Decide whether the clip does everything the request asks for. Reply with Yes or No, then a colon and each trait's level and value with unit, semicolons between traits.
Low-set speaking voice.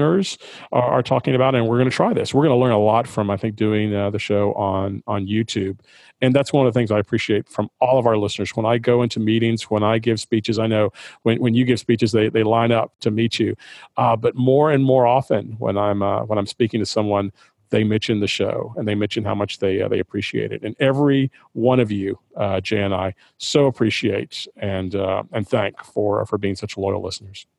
Yes: low, 110 Hz